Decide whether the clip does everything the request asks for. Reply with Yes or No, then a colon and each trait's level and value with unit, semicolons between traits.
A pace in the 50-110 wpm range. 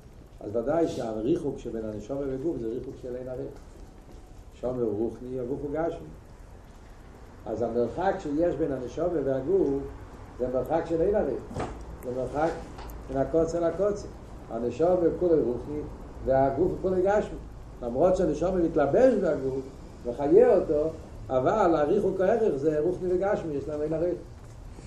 No: average, 135 wpm